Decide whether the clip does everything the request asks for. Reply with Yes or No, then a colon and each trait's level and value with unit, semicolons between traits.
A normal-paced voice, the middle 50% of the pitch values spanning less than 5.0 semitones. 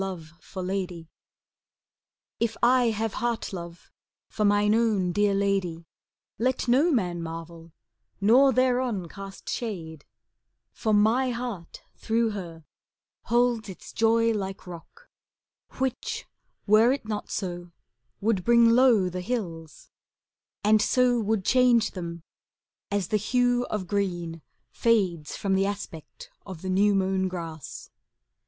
No: slow, 125 wpm; average, 4.5 semitones